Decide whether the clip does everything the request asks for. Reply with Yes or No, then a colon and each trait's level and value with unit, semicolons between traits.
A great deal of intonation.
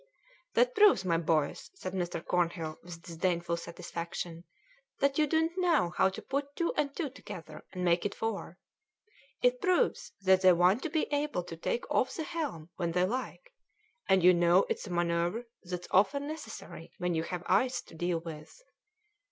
Yes: wide, 8.6 semitones